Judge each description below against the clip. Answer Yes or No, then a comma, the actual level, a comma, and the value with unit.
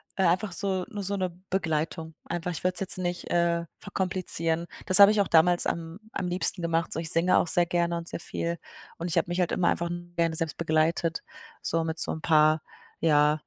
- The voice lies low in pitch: No, medium, 170 Hz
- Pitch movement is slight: Yes, narrow, 1.8 semitones